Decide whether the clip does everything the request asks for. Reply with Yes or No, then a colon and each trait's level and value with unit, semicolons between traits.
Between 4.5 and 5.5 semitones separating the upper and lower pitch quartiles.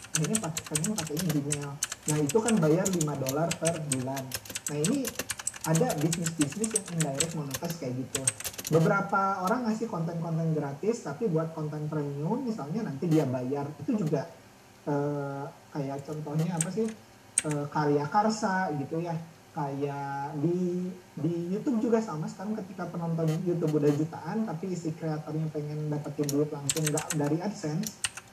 No: average, 3.8 semitones